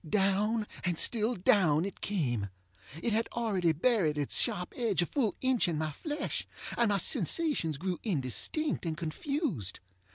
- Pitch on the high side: Yes, high, 195 Hz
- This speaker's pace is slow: No, average, 155 wpm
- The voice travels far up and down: Yes, wide, 6.9 semitones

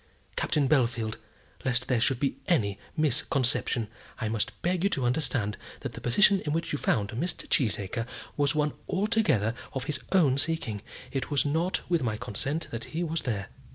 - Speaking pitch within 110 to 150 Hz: Yes, low, 135 Hz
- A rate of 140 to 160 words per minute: No, average, 175 wpm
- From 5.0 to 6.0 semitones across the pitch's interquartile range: Yes, wide, 5.6 semitones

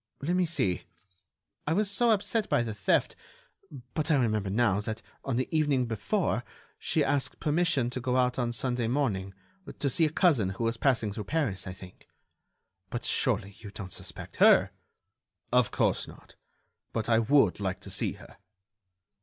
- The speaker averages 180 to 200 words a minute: No, average, 170 wpm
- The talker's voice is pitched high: No, low, 120 Hz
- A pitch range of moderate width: No, wide, 5.9 semitones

